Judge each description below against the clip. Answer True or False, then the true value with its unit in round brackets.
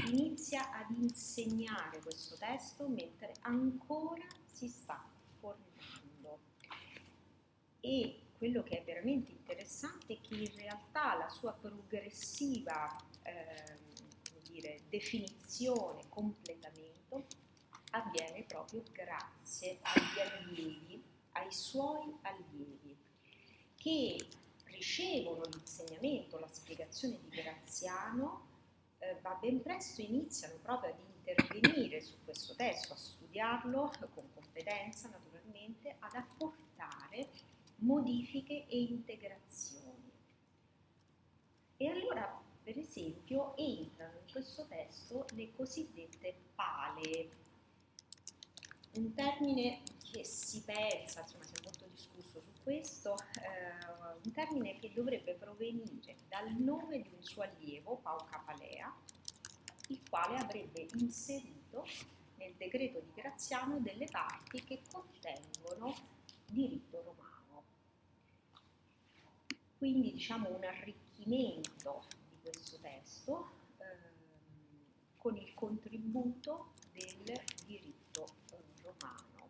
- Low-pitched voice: False (225 Hz)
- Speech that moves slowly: True (95 wpm)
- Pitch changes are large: True (7.7 semitones)